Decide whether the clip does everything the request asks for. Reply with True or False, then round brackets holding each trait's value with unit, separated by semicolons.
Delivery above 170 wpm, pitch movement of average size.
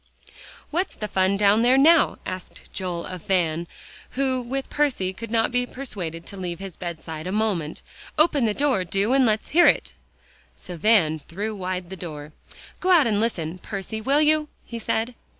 False (180 wpm; 5.9 semitones)